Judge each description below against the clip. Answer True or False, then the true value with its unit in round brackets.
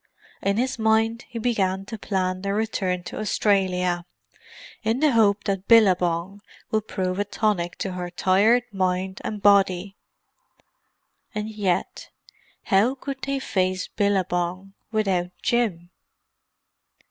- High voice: True (200 Hz)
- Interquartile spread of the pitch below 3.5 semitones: True (3.0 semitones)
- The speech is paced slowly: True (120 wpm)